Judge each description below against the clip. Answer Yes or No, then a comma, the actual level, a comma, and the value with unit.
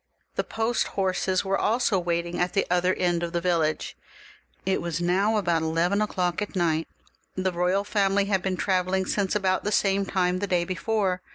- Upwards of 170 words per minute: Yes, average, 195 wpm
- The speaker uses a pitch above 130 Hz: Yes, medium, 185 Hz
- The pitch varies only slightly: Yes, narrow, 2.1 semitones